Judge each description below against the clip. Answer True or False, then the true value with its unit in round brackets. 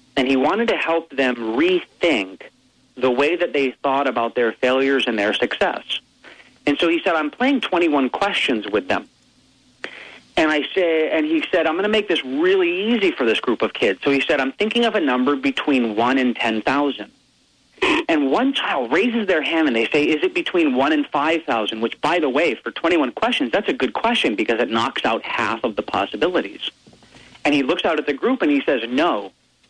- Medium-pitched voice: True (160 Hz)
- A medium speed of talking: False (215 wpm)